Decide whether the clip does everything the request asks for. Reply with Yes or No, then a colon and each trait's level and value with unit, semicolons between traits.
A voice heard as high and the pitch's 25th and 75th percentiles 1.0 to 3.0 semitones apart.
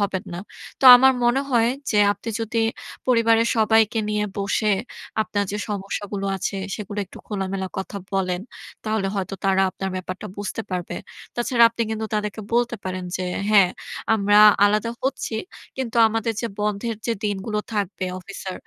Yes: high, 210 Hz; average, 2.7 semitones